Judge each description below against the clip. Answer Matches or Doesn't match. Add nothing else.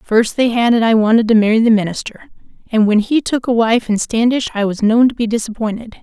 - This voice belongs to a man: Doesn't match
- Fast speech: Matches